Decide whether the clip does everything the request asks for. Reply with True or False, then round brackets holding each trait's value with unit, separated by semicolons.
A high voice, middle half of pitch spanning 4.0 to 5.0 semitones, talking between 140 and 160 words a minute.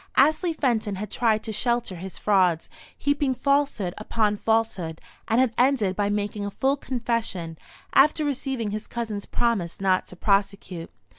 True (215 Hz; 4.4 semitones; 150 wpm)